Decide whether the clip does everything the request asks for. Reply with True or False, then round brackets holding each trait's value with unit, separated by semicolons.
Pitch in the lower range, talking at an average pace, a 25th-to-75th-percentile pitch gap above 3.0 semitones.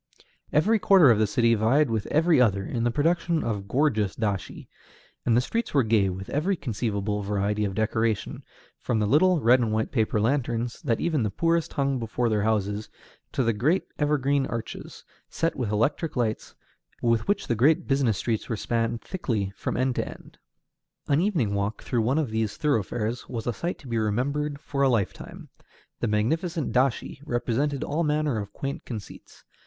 True (120 Hz; 180 wpm; 5.1 semitones)